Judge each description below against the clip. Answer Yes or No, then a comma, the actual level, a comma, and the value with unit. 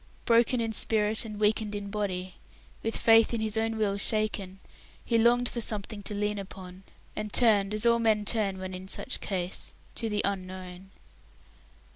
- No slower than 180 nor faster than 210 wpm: No, average, 170 wpm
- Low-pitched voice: No, high, 210 Hz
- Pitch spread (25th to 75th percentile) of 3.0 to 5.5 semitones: No, narrow, 2.5 semitones